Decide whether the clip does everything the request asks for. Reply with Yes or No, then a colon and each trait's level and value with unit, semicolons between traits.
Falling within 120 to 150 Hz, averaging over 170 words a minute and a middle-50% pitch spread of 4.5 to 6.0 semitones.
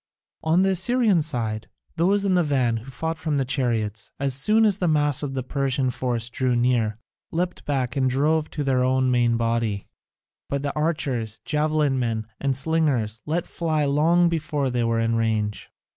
Yes: low, 135 Hz; average, 180 wpm; average, 4.9 semitones